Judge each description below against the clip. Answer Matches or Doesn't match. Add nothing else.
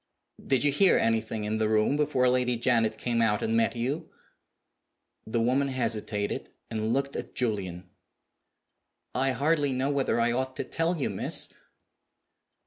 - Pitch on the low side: Matches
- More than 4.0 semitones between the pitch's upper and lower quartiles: Doesn't match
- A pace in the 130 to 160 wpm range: Matches